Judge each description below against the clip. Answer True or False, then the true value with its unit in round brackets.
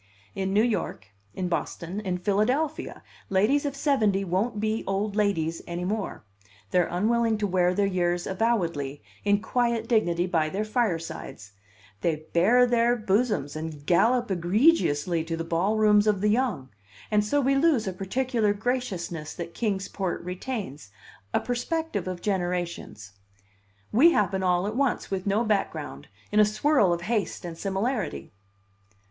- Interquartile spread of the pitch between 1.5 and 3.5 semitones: False (4.7 semitones)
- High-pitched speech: True (200 Hz)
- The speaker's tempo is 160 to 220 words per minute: False (150 wpm)